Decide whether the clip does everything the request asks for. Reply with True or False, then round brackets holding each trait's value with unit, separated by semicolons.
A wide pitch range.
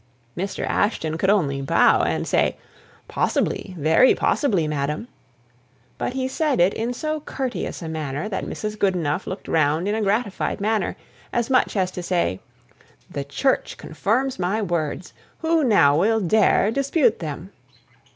True (6.8 semitones)